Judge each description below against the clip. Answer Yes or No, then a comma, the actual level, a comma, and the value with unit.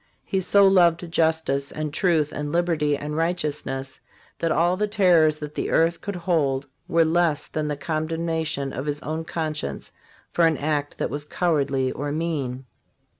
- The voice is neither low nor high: Yes, medium, 155 Hz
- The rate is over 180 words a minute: No, average, 170 wpm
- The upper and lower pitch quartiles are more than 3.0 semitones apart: No, narrow, 2.5 semitones